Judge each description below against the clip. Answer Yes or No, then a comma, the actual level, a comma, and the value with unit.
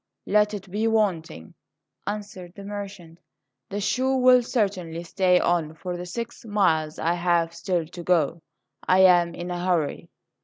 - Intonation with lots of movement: No, average, 3.3 semitones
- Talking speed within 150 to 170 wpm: Yes, average, 155 wpm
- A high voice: No, medium, 180 Hz